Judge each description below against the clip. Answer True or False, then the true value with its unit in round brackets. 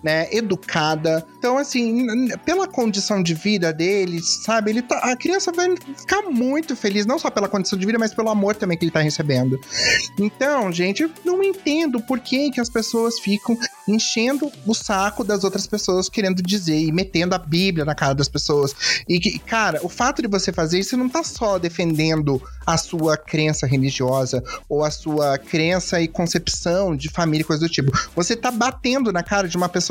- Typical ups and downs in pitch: False (6.8 semitones)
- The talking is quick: True (195 wpm)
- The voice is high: True (195 Hz)